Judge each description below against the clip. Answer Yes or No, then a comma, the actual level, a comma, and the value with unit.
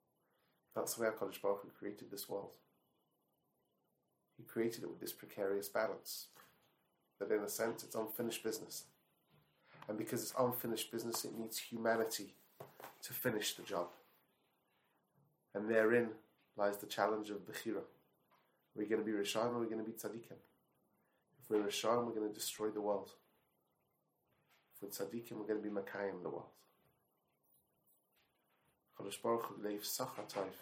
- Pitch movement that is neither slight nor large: No, narrow, 1.8 semitones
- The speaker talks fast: No, average, 140 wpm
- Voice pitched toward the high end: No, low, 110 Hz